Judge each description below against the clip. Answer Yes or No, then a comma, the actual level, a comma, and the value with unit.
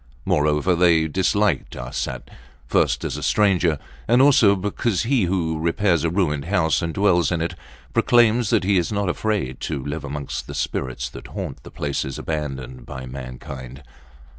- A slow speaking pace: No, average, 165 wpm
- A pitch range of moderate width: No, wide, 5.8 semitones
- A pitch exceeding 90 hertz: No, very low, 85 Hz